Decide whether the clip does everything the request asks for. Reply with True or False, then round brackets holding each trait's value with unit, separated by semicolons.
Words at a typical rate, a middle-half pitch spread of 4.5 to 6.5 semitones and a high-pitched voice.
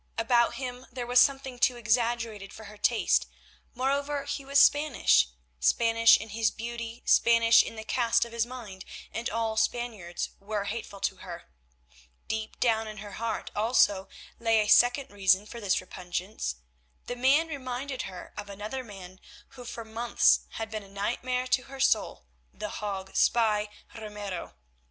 False (160 wpm; 2.9 semitones; 230 Hz)